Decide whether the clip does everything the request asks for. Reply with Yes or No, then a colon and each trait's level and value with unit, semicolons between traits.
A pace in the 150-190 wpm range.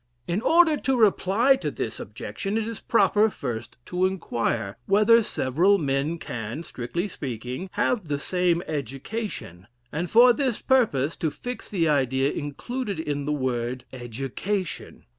No: average, 140 wpm